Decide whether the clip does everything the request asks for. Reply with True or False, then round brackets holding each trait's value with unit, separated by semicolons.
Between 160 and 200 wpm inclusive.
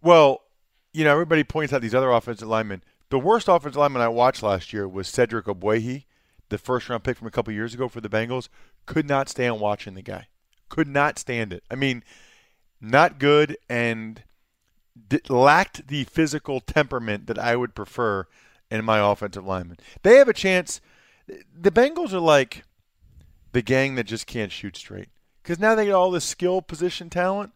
True (185 wpm)